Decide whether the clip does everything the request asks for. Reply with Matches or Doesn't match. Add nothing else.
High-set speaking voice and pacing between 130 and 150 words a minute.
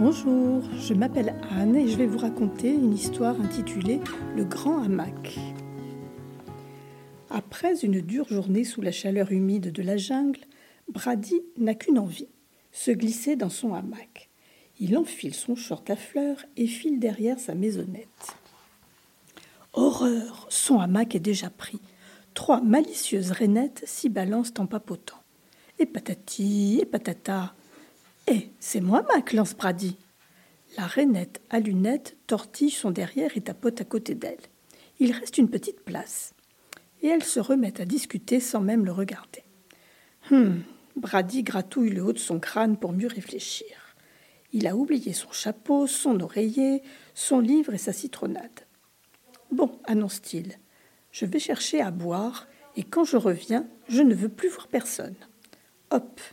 Matches